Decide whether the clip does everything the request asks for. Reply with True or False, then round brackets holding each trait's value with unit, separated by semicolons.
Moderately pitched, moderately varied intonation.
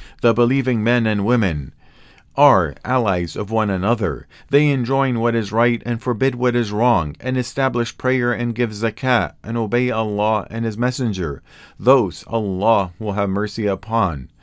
False (115 Hz; 3.0 semitones)